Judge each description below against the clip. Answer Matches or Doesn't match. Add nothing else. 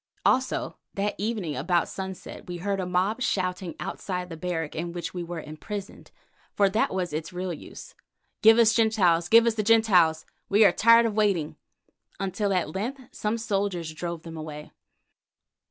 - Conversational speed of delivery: Matches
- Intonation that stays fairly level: Doesn't match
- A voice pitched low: Doesn't match